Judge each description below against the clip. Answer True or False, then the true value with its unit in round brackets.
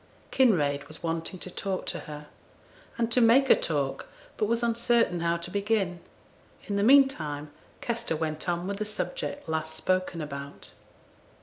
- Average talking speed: True (160 wpm)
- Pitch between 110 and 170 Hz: False (185 Hz)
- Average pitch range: False (6.5 semitones)